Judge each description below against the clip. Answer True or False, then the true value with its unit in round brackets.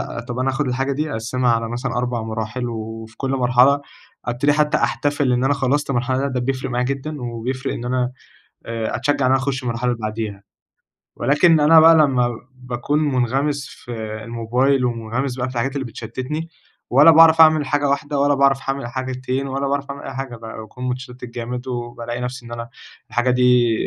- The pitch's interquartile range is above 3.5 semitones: False (2.5 semitones)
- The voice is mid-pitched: False (130 Hz)